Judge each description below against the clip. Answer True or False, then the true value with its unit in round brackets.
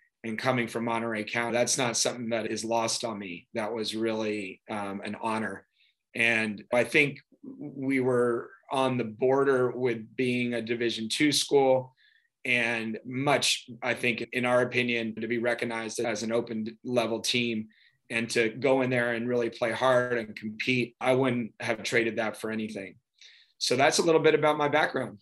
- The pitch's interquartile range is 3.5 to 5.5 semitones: False (2.4 semitones)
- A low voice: True (120 Hz)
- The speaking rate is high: False (175 wpm)